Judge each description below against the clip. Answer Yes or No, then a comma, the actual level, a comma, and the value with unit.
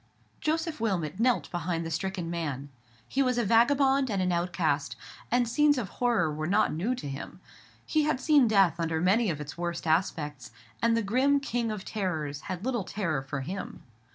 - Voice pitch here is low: No, high, 190 Hz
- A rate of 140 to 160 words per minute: No, average, 185 wpm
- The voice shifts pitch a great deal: Yes, wide, 6.9 semitones